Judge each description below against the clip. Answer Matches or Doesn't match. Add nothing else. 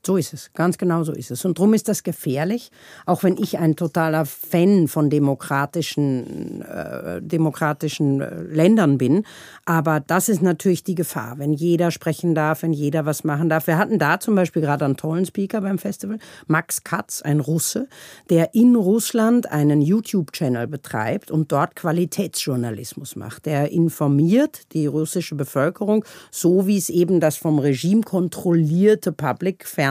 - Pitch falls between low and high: Matches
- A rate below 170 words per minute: Matches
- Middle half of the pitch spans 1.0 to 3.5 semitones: Doesn't match